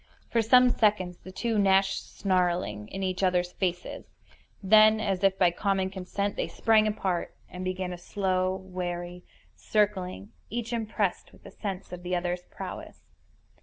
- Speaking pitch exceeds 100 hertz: Yes, high, 190 Hz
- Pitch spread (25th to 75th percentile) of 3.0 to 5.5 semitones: No, narrow, 2.5 semitones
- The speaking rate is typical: Yes, average, 155 wpm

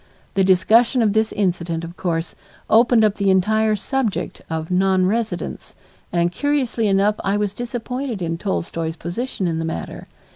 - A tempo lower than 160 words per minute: Yes, average, 150 wpm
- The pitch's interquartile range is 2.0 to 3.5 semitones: No, average, 4.3 semitones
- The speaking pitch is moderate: No, high, 200 Hz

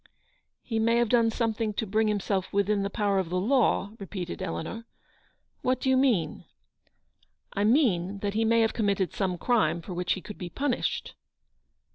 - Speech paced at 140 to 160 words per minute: No, average, 195 wpm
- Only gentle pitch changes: No, average, 3.3 semitones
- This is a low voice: No, high, 210 Hz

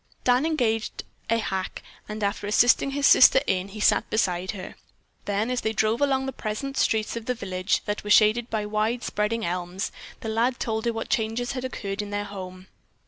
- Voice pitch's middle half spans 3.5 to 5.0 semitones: No, average, 3.0 semitones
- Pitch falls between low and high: No, high, 220 Hz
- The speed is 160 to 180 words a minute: No, average, 195 wpm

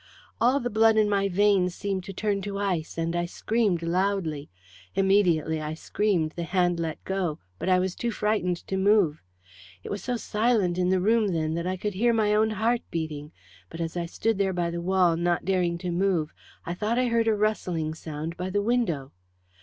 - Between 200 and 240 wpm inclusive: Yes, fast, 205 wpm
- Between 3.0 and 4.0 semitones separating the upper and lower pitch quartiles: Yes, average, 3.6 semitones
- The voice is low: No, medium, 185 Hz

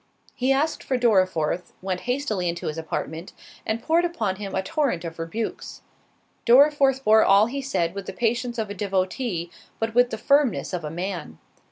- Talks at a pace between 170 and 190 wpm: Yes, average, 180 wpm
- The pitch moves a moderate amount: No, wide, 6.0 semitones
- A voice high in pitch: Yes, high, 215 Hz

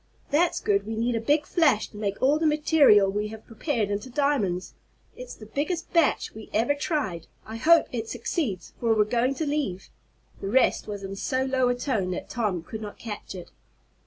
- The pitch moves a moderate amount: No, wide, 5.7 semitones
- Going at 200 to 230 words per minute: Yes, fast, 205 wpm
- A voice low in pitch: No, high, 230 Hz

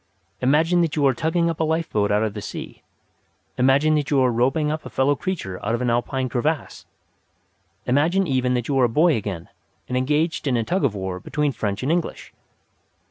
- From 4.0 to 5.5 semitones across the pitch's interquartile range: Yes, average, 4.9 semitones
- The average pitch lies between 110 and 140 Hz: Yes, low, 135 Hz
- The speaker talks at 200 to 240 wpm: Yes, fast, 205 wpm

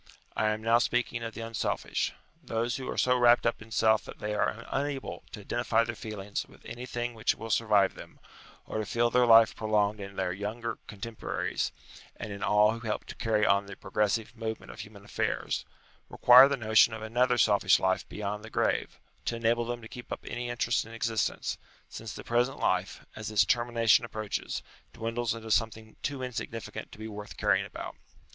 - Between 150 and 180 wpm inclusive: No, average, 195 wpm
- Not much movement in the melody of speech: Yes, narrow, 1.9 semitones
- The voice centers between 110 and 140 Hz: Yes, low, 115 Hz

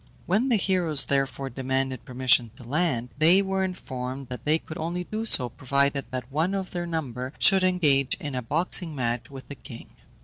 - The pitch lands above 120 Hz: Yes, medium, 140 Hz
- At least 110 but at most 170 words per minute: No, average, 190 wpm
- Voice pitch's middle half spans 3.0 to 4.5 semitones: No, wide, 5.5 semitones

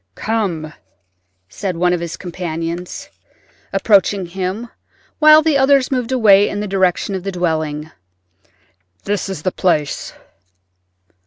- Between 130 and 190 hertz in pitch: Yes, medium, 185 Hz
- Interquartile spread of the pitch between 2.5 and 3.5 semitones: No, average, 4.4 semitones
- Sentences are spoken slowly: Yes, slow, 115 wpm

